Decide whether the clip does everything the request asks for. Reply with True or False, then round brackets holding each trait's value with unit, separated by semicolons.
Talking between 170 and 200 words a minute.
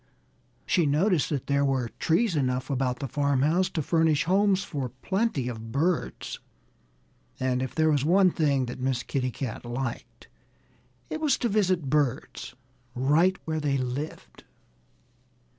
False (140 wpm)